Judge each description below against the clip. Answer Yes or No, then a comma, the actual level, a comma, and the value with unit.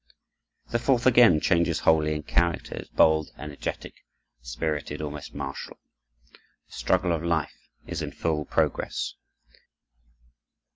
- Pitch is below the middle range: Yes, very low, 80 Hz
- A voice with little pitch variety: Yes, narrow, 2.2 semitones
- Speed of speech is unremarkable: No, slow, 115 wpm